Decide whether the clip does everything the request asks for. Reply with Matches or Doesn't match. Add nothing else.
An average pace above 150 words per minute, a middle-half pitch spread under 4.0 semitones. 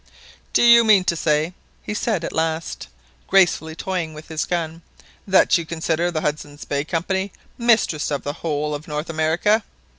Matches